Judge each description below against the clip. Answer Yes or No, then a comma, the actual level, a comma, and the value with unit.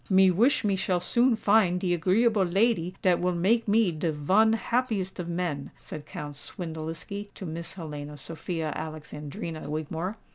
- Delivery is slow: No, average, 155 wpm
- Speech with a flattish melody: No, average, 4.4 semitones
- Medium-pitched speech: Yes, medium, 180 Hz